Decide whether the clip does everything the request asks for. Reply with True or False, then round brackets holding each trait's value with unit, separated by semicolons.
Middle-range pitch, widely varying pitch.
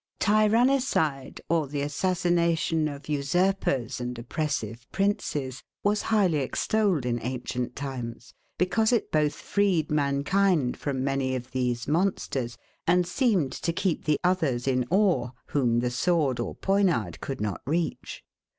True (150 Hz; 6.2 semitones)